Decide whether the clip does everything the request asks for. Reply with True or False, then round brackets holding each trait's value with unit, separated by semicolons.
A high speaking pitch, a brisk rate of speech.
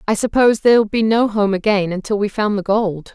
True (210 Hz; 230 wpm)